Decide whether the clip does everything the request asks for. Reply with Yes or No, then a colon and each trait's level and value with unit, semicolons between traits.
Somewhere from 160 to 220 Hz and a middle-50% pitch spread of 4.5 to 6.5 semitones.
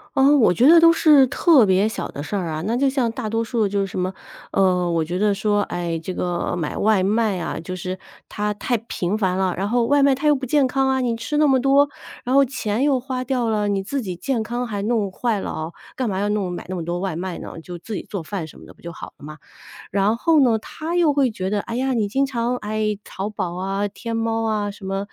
Yes: high, 215 Hz; average, 5.2 semitones